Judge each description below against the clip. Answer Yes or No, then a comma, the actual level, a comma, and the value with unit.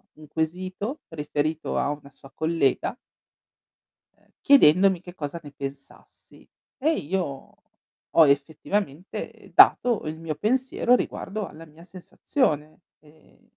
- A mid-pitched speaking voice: Yes, medium, 160 Hz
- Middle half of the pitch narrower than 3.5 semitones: No, average, 4.5 semitones